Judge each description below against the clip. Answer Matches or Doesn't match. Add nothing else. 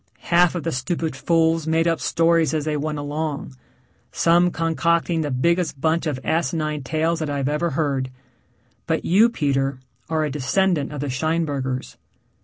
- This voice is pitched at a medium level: Matches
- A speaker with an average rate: Matches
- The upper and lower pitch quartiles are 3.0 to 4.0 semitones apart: Doesn't match